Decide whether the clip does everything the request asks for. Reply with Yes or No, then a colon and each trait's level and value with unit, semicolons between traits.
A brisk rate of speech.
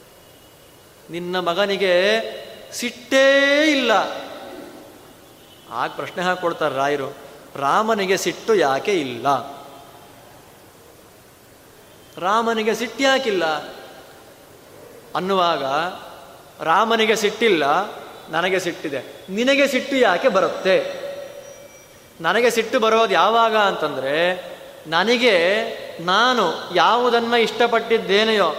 No: average, 70 wpm